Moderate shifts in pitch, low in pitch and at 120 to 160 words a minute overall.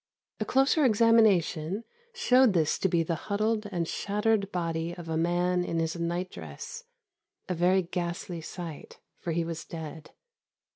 No: average, 3.9 semitones; medium, 175 Hz; average, 150 wpm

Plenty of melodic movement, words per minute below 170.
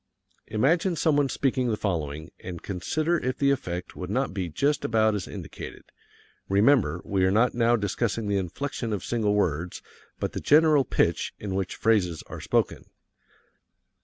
Yes: wide, 6.4 semitones; average, 160 wpm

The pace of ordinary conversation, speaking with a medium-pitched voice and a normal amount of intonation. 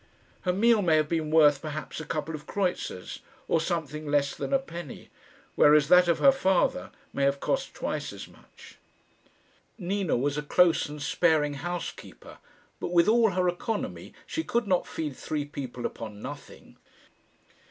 Yes: average, 165 wpm; medium, 160 Hz; average, 3.7 semitones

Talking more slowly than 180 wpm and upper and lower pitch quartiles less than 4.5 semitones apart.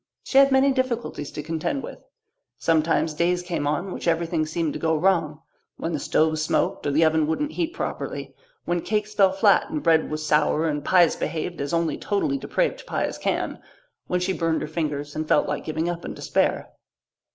No: average, 195 wpm; average, 3.8 semitones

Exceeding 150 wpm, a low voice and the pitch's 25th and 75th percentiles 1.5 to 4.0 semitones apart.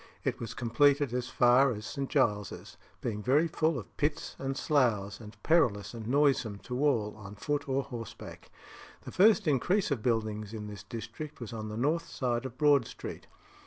No: average, 180 wpm; low, 125 Hz; average, 4.9 semitones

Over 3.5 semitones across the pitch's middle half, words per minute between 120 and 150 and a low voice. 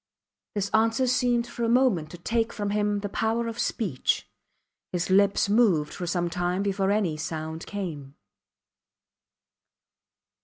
No: average, 4.5 semitones; average, 140 wpm; high, 200 Hz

